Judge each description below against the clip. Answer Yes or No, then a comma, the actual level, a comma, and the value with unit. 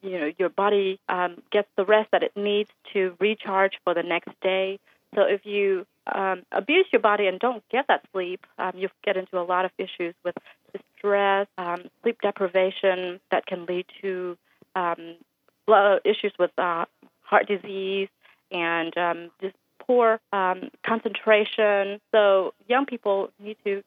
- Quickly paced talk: No, average, 160 wpm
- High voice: Yes, high, 195 Hz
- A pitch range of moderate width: No, narrow, 2.3 semitones